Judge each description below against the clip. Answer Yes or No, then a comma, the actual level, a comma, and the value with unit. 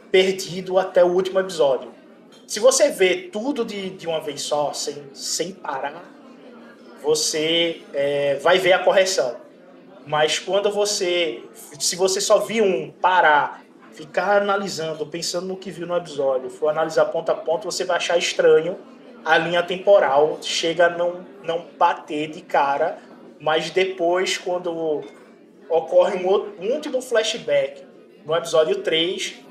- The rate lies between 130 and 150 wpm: Yes, average, 145 wpm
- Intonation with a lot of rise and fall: No, average, 3.5 semitones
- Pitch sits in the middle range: Yes, medium, 180 Hz